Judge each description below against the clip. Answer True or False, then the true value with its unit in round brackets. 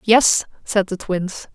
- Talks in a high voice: True (200 Hz)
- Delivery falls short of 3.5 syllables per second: True (3.3 syllables/s)